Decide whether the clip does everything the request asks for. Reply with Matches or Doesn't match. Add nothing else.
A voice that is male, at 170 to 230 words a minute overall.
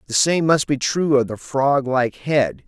Matches